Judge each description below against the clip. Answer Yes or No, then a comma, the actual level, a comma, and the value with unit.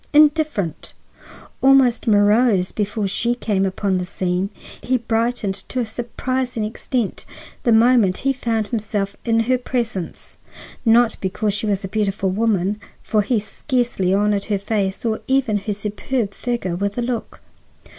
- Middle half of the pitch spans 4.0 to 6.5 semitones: No, average, 3.4 semitones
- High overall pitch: Yes, high, 215 Hz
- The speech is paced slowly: No, average, 145 wpm